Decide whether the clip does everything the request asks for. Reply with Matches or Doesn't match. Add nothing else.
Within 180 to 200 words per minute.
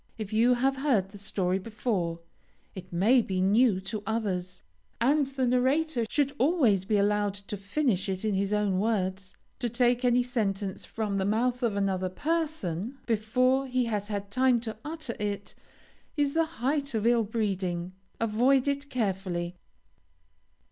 Doesn't match